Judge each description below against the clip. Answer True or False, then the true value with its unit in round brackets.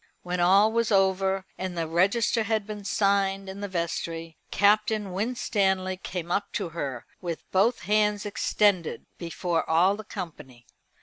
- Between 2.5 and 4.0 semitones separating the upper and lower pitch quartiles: True (3.0 semitones)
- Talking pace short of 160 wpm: True (145 wpm)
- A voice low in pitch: False (195 Hz)